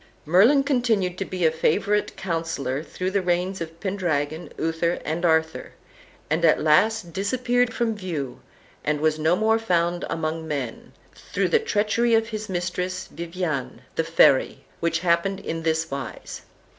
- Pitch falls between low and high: Yes, medium, 175 Hz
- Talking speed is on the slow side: No, average, 150 wpm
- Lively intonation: No, average, 4.0 semitones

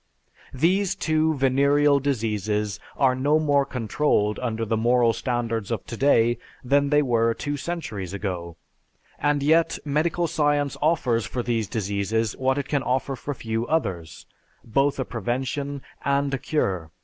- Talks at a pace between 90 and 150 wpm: Yes, average, 145 wpm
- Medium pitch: No, low, 130 Hz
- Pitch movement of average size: Yes, average, 4.3 semitones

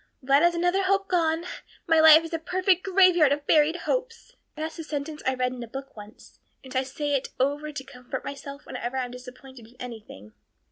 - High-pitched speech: Yes, very high, 290 Hz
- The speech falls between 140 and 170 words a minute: No, fast, 205 wpm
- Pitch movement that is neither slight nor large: Yes, average, 4.4 semitones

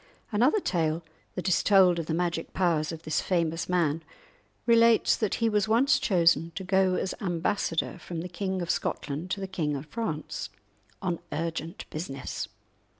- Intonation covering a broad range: No, average, 3.0 semitones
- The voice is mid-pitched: Yes, medium, 175 Hz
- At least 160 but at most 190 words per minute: Yes, average, 165 wpm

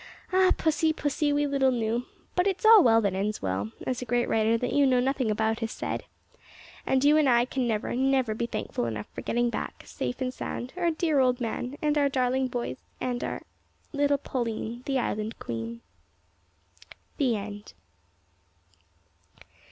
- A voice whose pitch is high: Yes, very high, 250 Hz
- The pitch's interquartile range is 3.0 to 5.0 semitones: Yes, average, 4.1 semitones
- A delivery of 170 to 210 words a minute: Yes, average, 175 wpm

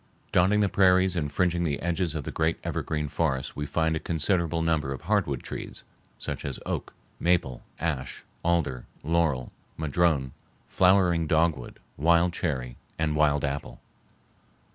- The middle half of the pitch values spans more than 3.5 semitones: No, average, 3.1 semitones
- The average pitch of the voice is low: Yes, very low, 80 Hz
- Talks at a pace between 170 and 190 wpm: No, average, 145 wpm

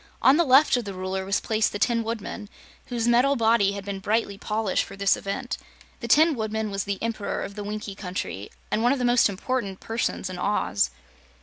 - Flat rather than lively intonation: No, average, 3.2 semitones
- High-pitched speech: Yes, high, 215 Hz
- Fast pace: Yes, fast, 210 wpm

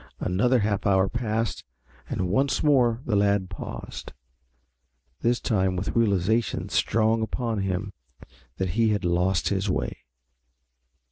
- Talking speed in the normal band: No, slow, 130 wpm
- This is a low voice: Yes, low, 105 Hz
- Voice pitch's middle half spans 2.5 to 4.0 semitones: Yes, average, 3.4 semitones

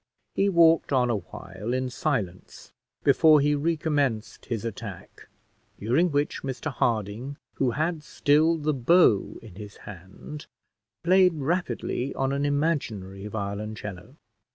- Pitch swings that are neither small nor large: No, wide, 6.3 semitones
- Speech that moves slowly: Yes, slow, 120 wpm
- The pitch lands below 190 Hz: Yes, low, 135 Hz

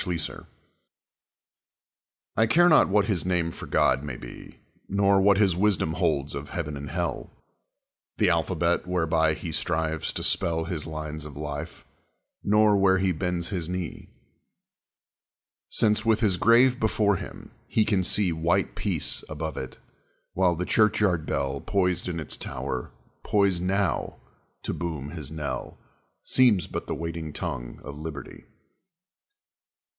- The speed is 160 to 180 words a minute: No, average, 145 wpm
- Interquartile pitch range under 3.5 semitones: No, average, 4.1 semitones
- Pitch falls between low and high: No, very low, 85 Hz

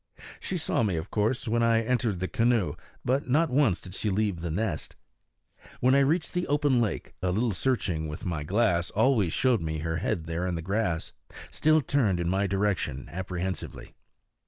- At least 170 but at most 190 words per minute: Yes, average, 185 wpm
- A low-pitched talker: Yes, low, 105 Hz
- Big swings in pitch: Yes, wide, 6.1 semitones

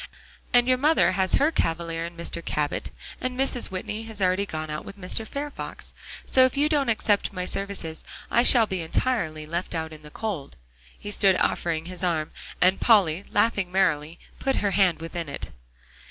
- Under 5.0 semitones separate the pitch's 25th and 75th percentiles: No, wide, 5.4 semitones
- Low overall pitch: No, medium, 185 Hz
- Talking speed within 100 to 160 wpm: No, average, 185 wpm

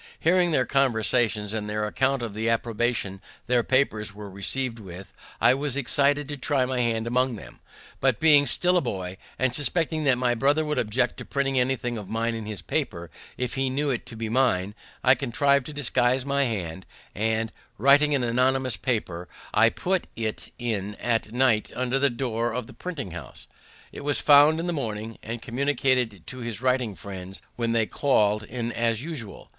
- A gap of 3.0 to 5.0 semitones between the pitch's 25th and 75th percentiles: Yes, average, 3.7 semitones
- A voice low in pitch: Yes, low, 120 Hz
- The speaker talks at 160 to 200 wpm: Yes, average, 185 wpm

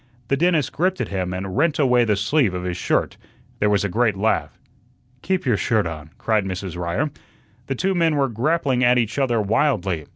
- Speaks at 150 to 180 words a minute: No, average, 200 wpm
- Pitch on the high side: No, low, 115 Hz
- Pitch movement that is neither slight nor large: No, wide, 6.7 semitones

